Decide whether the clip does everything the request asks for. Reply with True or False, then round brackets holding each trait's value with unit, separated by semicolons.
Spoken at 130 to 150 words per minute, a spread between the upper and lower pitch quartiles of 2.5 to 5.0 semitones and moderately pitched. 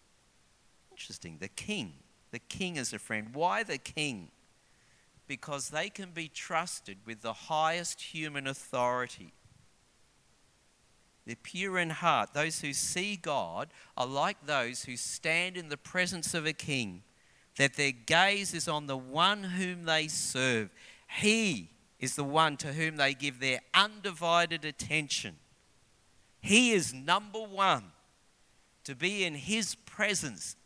False (135 wpm; 5.4 semitones; 155 Hz)